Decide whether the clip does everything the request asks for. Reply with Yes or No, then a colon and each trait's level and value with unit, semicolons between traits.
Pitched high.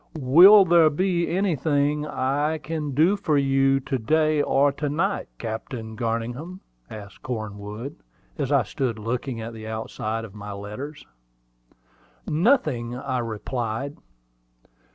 No: low, 135 Hz